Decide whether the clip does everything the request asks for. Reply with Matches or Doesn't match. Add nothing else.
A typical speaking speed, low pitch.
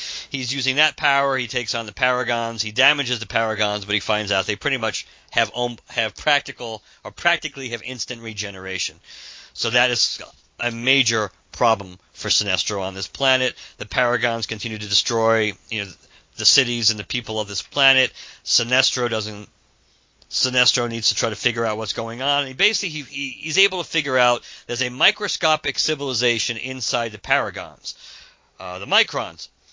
Matches